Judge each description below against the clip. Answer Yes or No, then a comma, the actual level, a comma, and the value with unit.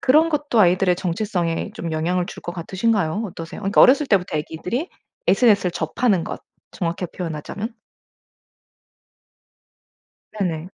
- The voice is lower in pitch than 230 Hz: Yes, medium, 185 Hz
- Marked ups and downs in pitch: No, average, 4.9 semitones